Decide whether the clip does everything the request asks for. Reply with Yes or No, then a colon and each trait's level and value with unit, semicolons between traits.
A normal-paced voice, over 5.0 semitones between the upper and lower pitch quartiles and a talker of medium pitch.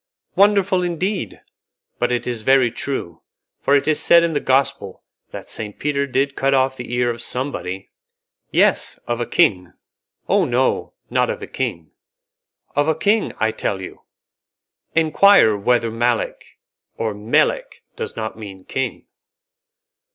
No: average, 145 wpm; wide, 5.5 semitones; low, 130 Hz